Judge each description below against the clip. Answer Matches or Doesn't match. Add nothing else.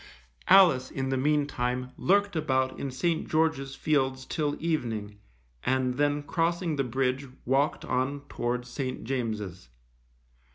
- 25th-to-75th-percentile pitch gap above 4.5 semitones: Doesn't match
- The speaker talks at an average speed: Doesn't match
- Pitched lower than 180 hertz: Matches